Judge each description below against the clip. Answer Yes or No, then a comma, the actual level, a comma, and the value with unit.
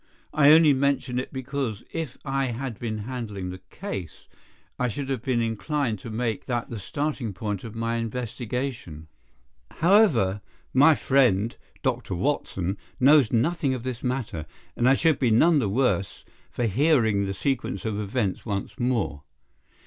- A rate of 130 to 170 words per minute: Yes, average, 155 wpm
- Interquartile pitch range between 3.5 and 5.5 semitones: Yes, average, 4.4 semitones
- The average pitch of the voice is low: Yes, low, 120 Hz